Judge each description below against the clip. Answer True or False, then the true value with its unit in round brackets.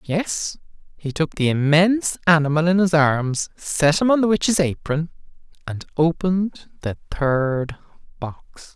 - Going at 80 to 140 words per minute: True (135 wpm)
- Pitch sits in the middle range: True (160 Hz)